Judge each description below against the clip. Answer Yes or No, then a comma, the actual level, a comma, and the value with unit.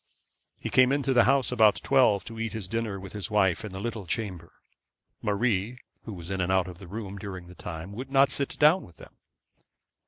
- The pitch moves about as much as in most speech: Yes, average, 4.4 semitones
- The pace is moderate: No, fast, 215 wpm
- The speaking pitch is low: Yes, low, 105 Hz